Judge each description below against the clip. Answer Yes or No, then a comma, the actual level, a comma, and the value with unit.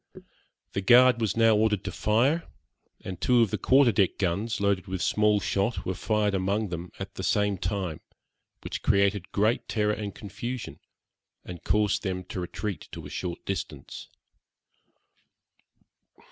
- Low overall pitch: Yes, low, 100 Hz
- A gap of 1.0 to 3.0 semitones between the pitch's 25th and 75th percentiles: Yes, narrow, 2.5 semitones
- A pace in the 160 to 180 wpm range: No, average, 150 wpm